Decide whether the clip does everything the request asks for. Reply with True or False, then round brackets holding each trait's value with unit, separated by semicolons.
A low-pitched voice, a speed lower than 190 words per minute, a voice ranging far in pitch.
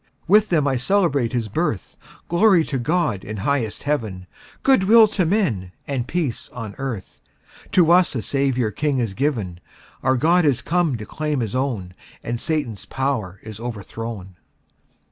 True (130 Hz; 160 wpm; 6.6 semitones)